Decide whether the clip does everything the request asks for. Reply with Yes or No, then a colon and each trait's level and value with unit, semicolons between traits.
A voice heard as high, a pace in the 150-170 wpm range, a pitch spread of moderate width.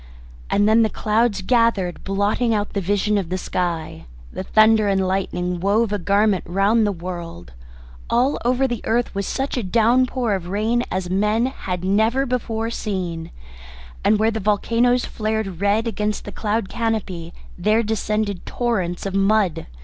Yes: high, 210 Hz; average, 160 wpm; average, 3.2 semitones